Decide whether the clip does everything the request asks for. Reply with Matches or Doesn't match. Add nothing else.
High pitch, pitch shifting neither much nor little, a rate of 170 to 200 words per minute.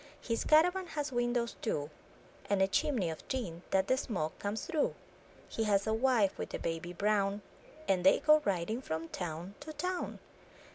Doesn't match